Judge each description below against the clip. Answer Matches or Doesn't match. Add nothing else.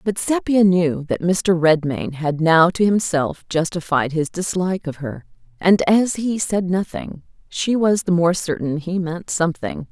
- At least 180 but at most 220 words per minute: Doesn't match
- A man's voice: Doesn't match